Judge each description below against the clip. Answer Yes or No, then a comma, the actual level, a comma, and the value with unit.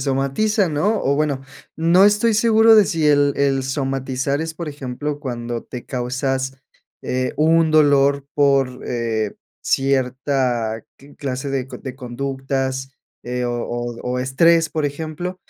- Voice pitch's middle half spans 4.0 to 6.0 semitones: No, average, 3.3 semitones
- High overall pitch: No, low, 135 Hz